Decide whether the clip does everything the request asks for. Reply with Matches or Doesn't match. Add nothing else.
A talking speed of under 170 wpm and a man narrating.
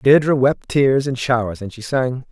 Doesn't match